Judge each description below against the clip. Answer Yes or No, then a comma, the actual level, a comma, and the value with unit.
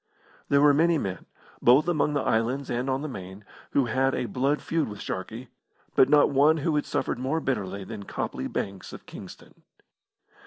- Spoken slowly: No, average, 185 wpm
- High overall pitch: No, low, 130 Hz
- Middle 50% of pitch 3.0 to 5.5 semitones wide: Yes, average, 5.0 semitones